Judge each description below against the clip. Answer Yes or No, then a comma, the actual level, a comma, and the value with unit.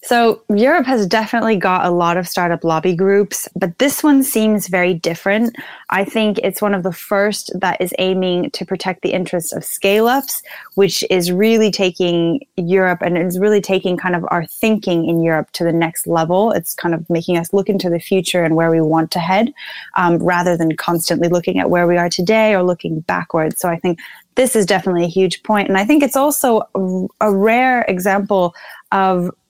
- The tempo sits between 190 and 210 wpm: Yes, average, 200 wpm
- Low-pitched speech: No, medium, 185 Hz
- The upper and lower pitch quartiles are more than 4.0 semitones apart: No, average, 3.3 semitones